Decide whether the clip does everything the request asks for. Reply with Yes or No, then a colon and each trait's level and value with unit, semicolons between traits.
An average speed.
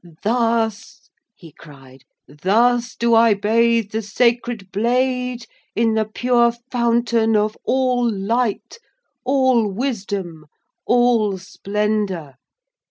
No: slow, 100 wpm